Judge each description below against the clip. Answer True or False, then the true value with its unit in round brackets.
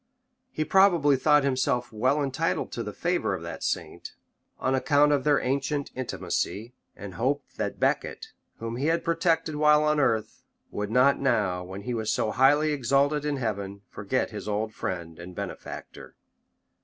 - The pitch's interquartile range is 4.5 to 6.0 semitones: True (5.2 semitones)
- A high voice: False (135 Hz)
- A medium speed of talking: True (165 wpm)